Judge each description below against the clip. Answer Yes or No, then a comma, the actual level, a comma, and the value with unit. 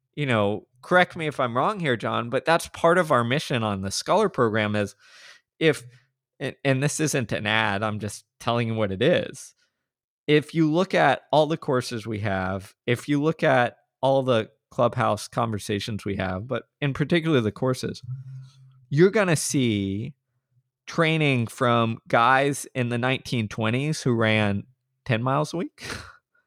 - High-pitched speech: No, low, 130 Hz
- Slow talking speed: No, average, 170 wpm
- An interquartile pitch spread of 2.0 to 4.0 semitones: No, average, 4.9 semitones